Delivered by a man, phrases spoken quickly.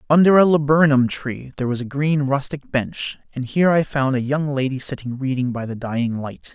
Yes: male; fast, 210 wpm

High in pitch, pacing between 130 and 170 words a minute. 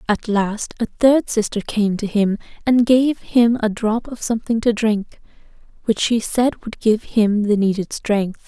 No: high, 220 Hz; average, 185 wpm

